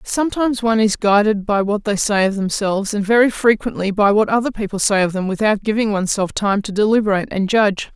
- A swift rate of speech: Yes, fast, 210 wpm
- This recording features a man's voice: No, female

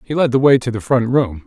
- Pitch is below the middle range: Yes, low, 125 Hz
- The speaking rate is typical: No, fast, 330 wpm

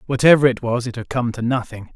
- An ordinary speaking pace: No, fast, 245 wpm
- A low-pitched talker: Yes, low, 120 Hz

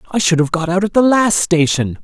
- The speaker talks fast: Yes, fast, 265 wpm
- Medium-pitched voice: Yes, medium, 175 Hz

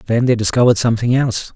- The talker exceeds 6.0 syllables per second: Yes, 8.0 syllables/s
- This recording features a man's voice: Yes, male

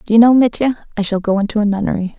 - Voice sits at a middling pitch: No, high, 215 Hz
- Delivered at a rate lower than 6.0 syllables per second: No, 7.1 syllables/s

